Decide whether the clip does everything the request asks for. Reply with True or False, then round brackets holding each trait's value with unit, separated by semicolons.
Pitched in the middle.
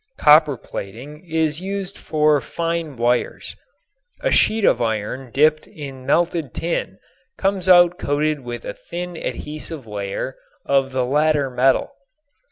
True (150 Hz)